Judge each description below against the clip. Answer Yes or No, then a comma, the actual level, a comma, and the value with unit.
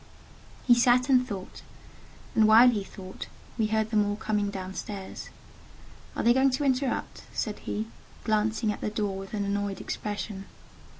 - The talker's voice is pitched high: Yes, high, 215 Hz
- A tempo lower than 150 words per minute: No, average, 165 wpm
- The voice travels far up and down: No, average, 2.8 semitones